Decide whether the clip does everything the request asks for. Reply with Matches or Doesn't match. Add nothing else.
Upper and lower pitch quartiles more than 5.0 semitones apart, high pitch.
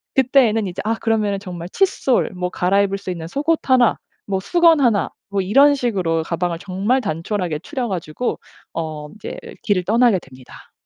Matches